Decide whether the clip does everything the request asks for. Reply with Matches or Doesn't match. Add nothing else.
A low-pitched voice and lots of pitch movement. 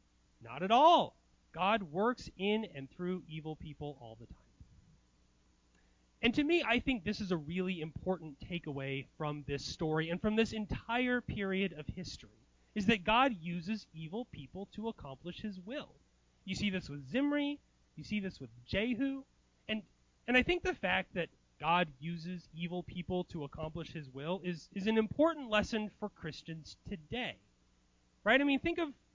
Doesn't match